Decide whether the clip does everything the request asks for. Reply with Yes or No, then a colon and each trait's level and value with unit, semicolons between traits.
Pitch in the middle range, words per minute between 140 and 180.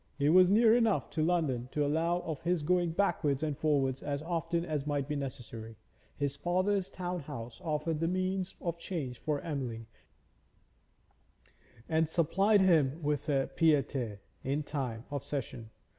Yes: medium, 150 Hz; average, 160 wpm